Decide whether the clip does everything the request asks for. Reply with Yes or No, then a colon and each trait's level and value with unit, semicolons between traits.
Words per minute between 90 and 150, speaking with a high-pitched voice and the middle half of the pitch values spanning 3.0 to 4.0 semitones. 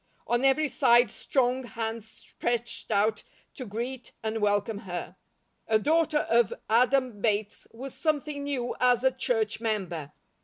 Yes: average, 140 wpm; high, 235 Hz; average, 3.3 semitones